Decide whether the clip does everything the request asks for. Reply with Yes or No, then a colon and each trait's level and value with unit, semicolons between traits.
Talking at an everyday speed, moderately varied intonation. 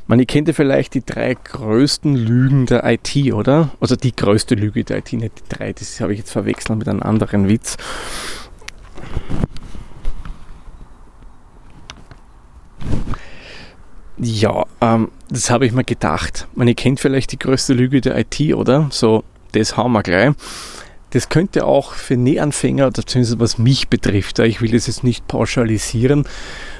Yes: average, 150 wpm; average, 3.5 semitones